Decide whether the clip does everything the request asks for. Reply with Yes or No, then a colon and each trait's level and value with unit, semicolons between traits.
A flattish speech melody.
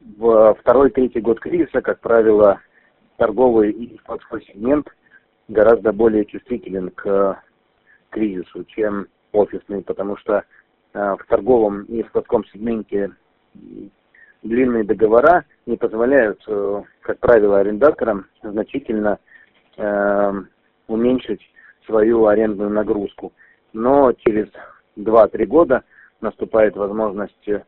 Yes: narrow, 2.2 semitones